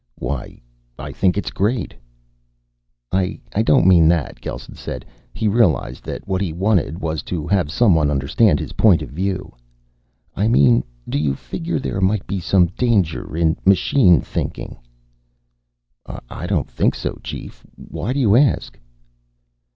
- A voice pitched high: No, very low, 90 Hz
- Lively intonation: No, average, 4.5 semitones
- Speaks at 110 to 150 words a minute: Yes, average, 145 wpm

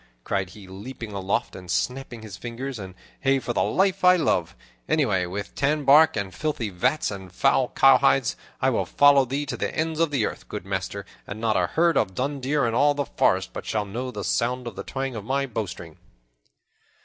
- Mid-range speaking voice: No, low, 120 Hz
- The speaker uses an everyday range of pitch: No, wide, 5.7 semitones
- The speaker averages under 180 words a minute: No, fast, 205 wpm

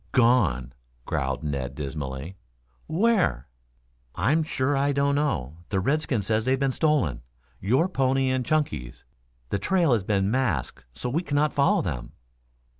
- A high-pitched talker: No, low, 125 Hz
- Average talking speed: Yes, average, 145 wpm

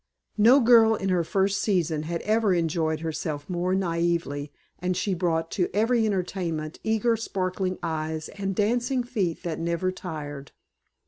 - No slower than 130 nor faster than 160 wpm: Yes, average, 145 wpm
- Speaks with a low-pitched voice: No, medium, 180 Hz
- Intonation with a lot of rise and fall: No, average, 4.1 semitones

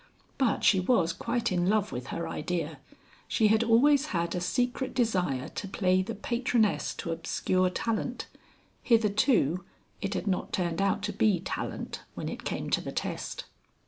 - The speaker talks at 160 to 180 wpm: Yes, average, 165 wpm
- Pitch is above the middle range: Yes, high, 195 Hz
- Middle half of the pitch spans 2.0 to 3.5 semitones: No, average, 4.5 semitones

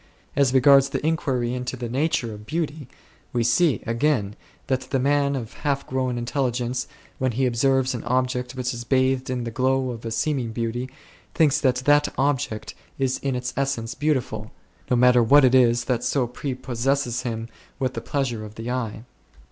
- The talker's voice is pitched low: Yes, low, 130 Hz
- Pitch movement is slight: Yes, narrow, 2.3 semitones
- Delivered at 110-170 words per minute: No, average, 180 wpm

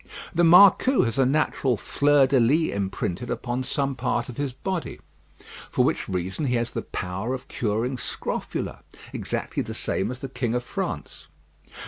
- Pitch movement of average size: Yes, average, 3.5 semitones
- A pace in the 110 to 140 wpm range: No, average, 165 wpm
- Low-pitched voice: Yes, low, 125 Hz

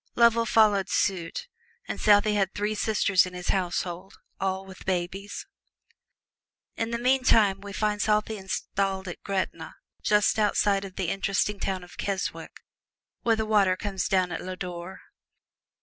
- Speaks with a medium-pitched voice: No, high, 195 Hz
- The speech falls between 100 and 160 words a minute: Yes, average, 150 wpm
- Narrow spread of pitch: Yes, narrow, 2.1 semitones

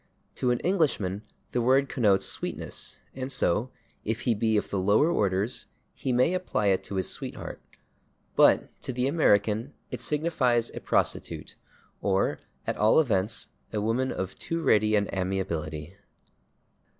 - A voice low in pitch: Yes, low, 110 Hz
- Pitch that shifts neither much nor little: Yes, average, 4.8 semitones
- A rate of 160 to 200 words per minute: No, average, 150 wpm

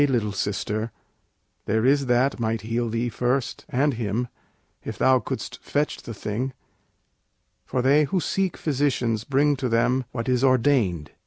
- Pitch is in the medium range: No, low, 125 Hz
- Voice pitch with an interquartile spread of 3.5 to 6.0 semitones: No, average, 3.1 semitones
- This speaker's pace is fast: No, average, 150 wpm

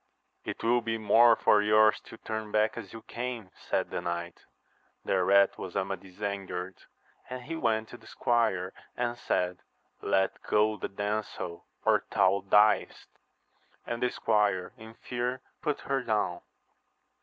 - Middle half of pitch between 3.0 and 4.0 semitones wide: Yes, average, 3.3 semitones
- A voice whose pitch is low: Yes, low, 110 Hz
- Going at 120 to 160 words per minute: Yes, average, 150 wpm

